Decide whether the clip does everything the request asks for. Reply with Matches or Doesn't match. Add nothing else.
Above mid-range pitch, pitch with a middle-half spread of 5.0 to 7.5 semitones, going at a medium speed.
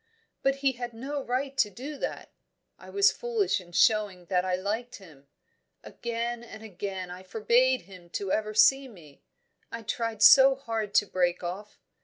Matches